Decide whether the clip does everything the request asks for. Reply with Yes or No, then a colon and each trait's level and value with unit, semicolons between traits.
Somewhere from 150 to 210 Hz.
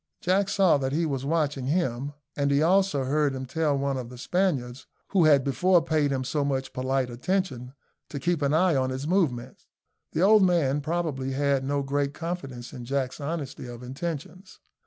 No: medium, 140 Hz